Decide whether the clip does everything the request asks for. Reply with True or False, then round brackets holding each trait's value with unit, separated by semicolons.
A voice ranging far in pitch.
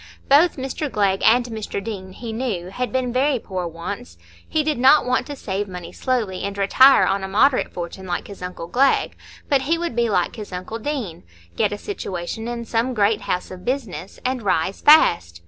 True (5.7 semitones)